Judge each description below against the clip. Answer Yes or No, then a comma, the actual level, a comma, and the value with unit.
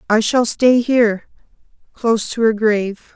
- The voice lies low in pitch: No, high, 225 Hz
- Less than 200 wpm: Yes, slow, 135 wpm